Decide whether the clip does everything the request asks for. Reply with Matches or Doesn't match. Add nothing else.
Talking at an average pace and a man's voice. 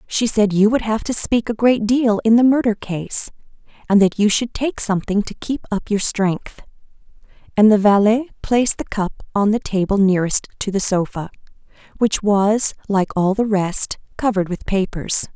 Doesn't match